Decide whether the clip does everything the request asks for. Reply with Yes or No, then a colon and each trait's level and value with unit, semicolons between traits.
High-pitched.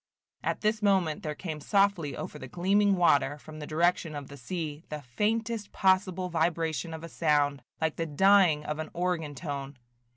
No: medium, 165 Hz